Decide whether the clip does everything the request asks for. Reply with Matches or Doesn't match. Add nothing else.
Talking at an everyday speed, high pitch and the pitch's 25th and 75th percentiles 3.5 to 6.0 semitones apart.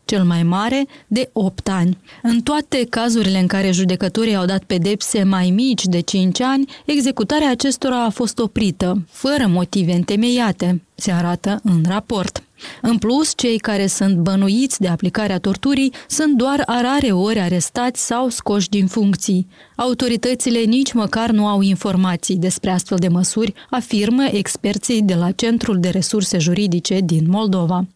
Matches